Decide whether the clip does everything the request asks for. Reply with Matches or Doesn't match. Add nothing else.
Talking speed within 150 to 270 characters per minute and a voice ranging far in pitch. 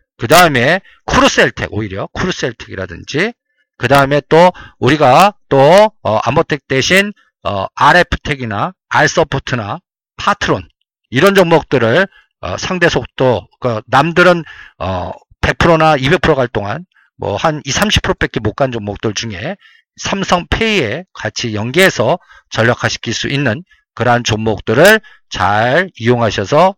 Matches